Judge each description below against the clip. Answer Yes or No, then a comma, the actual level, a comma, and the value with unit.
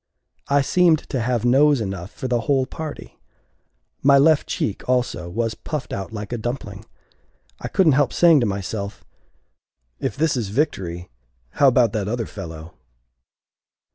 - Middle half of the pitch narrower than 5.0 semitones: No, wide, 5.6 semitones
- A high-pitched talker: No, low, 120 Hz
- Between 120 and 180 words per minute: Yes, average, 150 wpm